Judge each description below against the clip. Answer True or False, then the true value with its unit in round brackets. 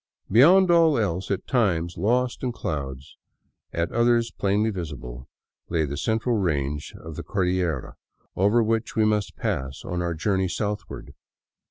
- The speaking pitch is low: True (95 Hz)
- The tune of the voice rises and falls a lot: True (5.7 semitones)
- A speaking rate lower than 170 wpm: True (145 wpm)